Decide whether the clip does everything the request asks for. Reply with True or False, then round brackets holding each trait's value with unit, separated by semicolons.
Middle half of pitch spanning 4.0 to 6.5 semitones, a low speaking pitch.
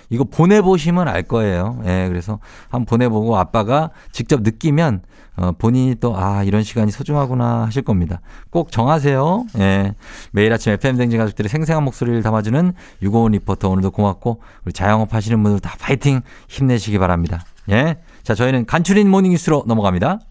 True (5.4 semitones; 115 Hz)